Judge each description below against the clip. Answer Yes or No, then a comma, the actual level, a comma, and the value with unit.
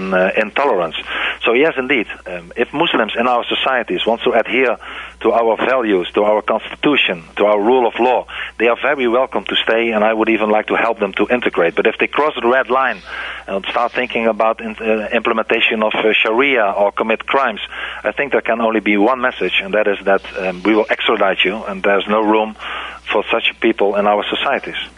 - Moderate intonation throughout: No, narrow, 1.5 semitones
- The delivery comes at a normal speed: No, fast, 215 wpm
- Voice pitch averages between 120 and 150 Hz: No, low, 110 Hz